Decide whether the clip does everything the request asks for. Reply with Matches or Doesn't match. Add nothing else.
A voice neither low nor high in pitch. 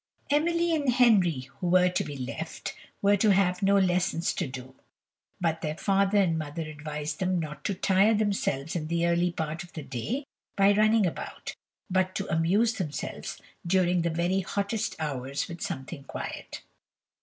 Matches